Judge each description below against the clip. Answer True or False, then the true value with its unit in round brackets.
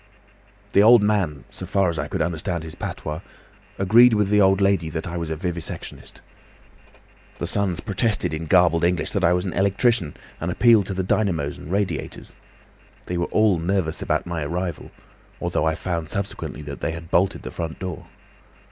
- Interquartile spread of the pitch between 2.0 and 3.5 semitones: True (3.2 semitones)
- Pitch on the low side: True (90 Hz)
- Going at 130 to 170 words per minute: False (185 wpm)